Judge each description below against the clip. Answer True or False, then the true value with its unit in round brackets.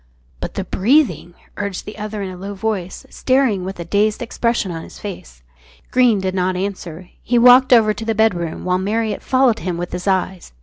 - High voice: True (200 Hz)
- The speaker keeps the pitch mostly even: False (3.6 semitones)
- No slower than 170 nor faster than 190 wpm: False (200 wpm)